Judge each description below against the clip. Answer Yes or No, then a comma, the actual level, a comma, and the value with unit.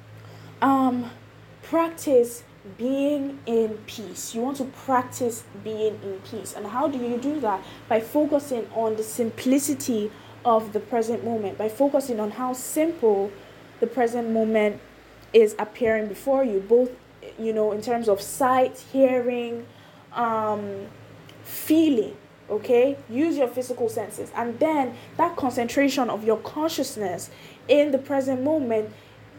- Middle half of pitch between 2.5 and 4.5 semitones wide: Yes, average, 3.8 semitones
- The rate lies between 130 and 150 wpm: Yes, slow, 135 wpm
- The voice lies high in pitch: Yes, high, 240 Hz